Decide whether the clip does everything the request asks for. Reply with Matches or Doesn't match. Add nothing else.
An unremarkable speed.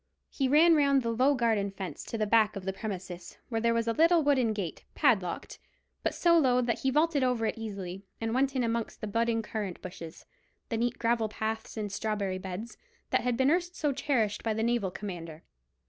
Doesn't match